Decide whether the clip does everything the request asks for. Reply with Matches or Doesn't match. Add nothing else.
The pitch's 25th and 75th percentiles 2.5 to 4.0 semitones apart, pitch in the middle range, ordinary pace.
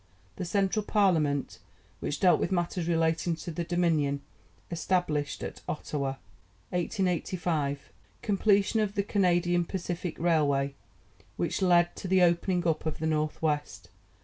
Doesn't match